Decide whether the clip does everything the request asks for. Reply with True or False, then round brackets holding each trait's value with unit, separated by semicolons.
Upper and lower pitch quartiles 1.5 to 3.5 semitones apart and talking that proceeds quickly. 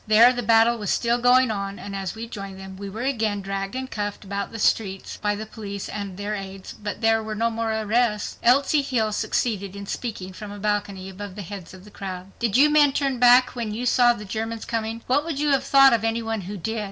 True (3.0 semitones; 240 wpm)